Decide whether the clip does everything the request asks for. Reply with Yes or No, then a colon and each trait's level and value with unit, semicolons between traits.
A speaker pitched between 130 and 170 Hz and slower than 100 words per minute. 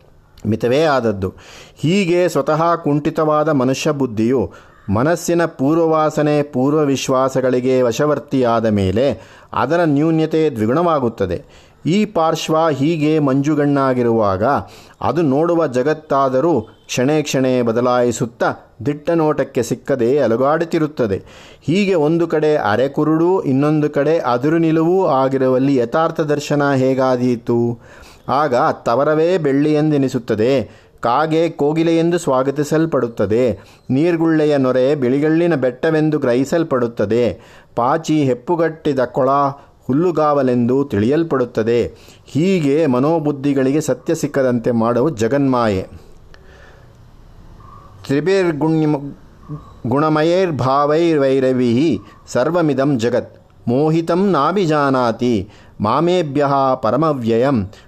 Yes: medium, 140 Hz; average, 75 wpm